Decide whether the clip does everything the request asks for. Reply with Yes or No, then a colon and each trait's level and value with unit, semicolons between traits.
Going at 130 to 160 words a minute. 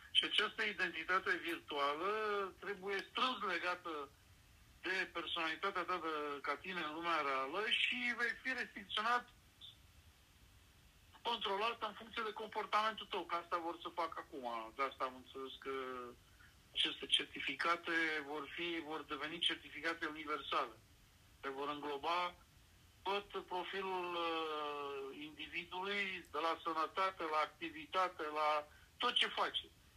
No: average, 120 wpm